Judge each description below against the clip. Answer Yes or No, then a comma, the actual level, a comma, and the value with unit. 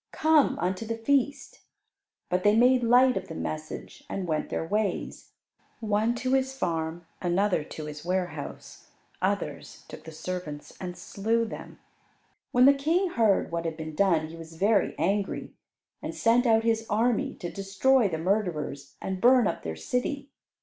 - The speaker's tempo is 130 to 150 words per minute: No, average, 165 wpm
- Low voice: No, high, 200 Hz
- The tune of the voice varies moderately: No, wide, 6.5 semitones